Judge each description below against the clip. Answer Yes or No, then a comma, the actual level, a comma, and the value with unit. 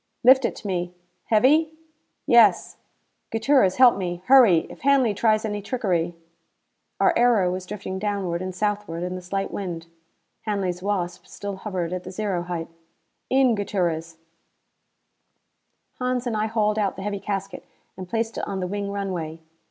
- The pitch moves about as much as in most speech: Yes, average, 3.5 semitones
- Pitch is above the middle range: Yes, high, 200 Hz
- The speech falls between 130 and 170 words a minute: Yes, average, 160 wpm